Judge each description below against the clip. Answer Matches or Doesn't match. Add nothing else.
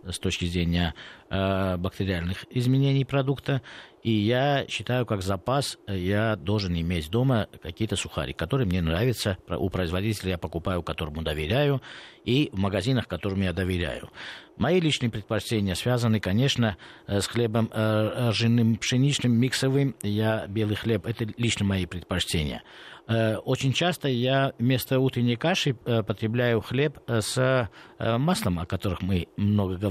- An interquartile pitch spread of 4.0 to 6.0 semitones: Matches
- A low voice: Matches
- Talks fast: Doesn't match